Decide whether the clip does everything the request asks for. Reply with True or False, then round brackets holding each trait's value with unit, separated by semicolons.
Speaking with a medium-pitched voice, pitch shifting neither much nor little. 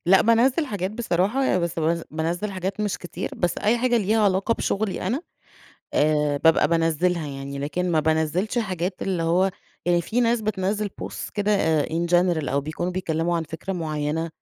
True (180 Hz; 4.0 semitones)